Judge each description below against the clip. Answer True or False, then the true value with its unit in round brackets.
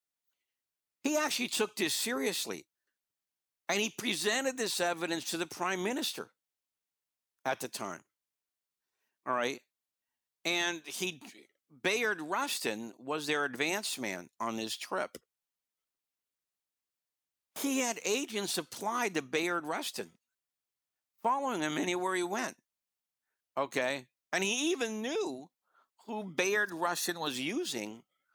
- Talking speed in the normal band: False (110 wpm)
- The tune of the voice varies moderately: False (8.2 semitones)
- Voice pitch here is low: False (175 Hz)